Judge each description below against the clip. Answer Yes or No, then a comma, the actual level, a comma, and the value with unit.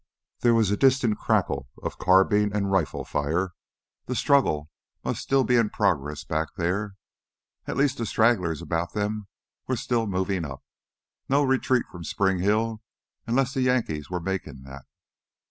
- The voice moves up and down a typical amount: No, wide, 5.7 semitones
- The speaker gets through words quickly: No, average, 155 wpm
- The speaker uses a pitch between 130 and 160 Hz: No, low, 100 Hz